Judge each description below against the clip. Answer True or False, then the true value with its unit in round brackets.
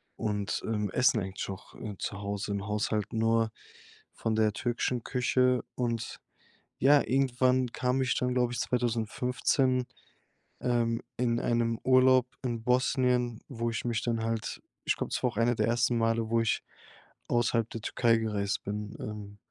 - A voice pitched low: True (115 Hz)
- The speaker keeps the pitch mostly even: True (2.2 semitones)